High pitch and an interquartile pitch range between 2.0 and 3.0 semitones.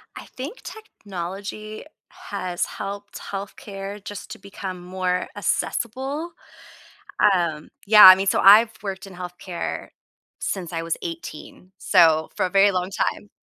Yes: high, 195 Hz; narrow, 2.4 semitones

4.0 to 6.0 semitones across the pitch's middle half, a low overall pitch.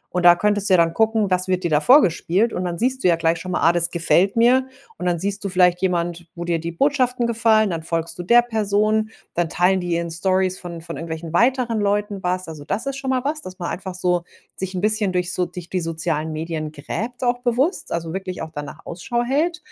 No: average, 4.6 semitones; medium, 185 Hz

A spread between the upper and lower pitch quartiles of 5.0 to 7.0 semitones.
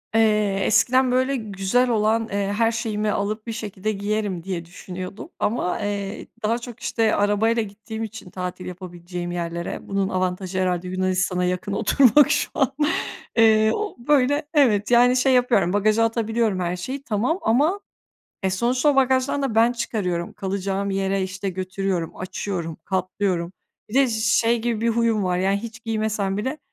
No: average, 3.8 semitones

